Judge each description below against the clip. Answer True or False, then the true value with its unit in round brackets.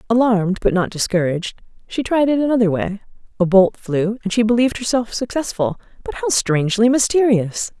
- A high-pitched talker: True (215 Hz)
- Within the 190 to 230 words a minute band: False (160 wpm)